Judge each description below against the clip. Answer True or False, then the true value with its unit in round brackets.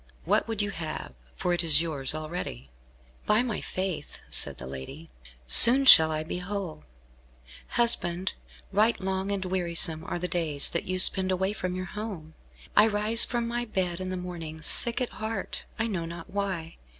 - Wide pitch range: False (4.1 semitones)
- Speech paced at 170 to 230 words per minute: True (175 wpm)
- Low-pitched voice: False (185 Hz)